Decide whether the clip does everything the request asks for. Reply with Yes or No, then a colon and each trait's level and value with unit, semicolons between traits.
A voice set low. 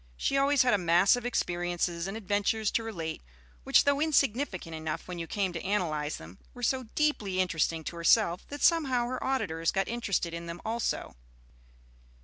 No: high, 195 Hz